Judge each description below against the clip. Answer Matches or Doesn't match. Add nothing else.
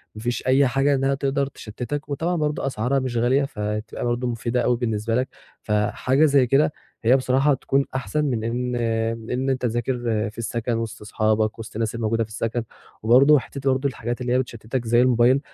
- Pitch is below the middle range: Matches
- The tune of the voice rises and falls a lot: Doesn't match